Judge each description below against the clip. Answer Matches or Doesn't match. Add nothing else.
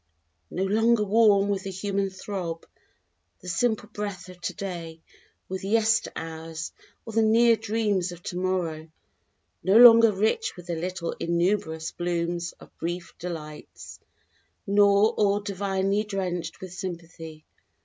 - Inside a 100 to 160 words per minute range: Matches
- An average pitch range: Matches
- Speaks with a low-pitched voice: Doesn't match